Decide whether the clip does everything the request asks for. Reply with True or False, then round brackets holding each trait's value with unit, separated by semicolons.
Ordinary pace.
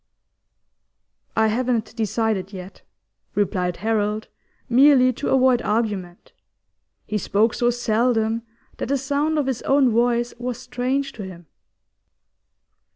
False (115 wpm)